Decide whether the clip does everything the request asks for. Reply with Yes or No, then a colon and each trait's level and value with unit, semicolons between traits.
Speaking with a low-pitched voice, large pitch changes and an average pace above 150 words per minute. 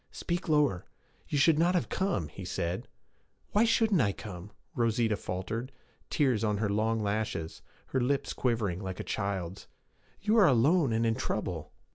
Yes: low, 115 Hz; wide, 6.9 semitones; average, 160 wpm